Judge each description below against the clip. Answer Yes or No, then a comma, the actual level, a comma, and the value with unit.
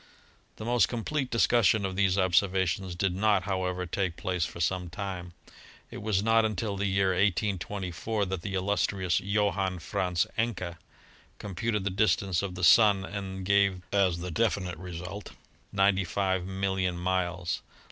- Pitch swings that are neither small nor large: No, narrow, 1.9 semitones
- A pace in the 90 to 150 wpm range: Yes, average, 140 wpm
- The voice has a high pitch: No, very low, 95 Hz